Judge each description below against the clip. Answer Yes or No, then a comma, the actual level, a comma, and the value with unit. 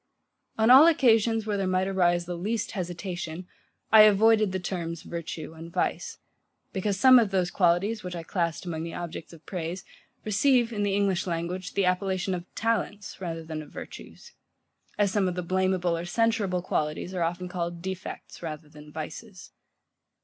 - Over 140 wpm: Yes, average, 170 wpm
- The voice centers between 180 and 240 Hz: Yes, medium, 185 Hz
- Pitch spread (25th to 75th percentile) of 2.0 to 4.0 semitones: Yes, average, 3.2 semitones